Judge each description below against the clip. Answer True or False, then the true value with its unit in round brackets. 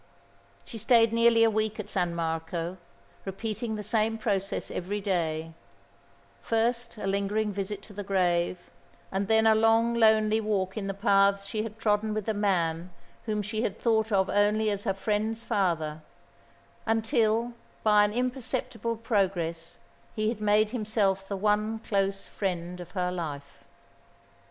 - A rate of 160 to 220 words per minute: False (150 wpm)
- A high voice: True (210 Hz)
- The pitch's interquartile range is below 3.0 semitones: True (2.6 semitones)